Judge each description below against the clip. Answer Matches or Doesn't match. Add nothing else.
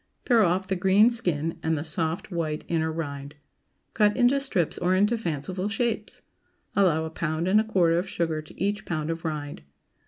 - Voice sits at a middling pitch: Matches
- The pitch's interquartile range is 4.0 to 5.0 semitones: Matches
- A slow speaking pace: Doesn't match